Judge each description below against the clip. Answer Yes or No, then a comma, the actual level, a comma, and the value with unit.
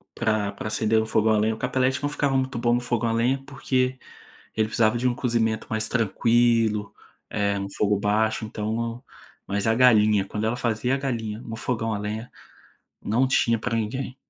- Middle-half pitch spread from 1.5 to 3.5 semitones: Yes, narrow, 2.4 semitones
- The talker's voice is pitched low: Yes, low, 115 Hz